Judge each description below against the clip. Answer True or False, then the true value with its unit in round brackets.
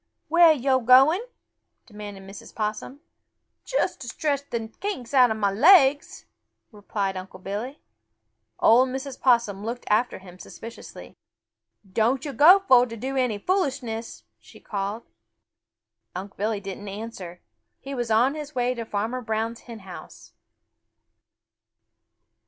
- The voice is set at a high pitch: True (230 Hz)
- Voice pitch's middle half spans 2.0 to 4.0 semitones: False (4.4 semitones)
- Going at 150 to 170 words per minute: False (135 wpm)